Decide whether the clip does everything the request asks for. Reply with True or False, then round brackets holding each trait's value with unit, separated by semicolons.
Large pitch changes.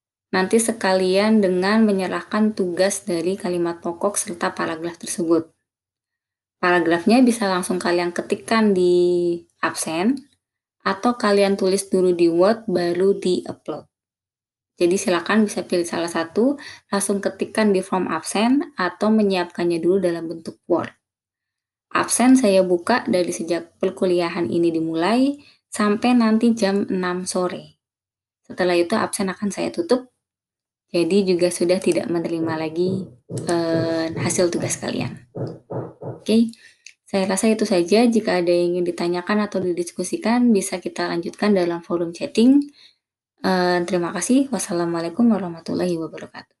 False (3.2 semitones)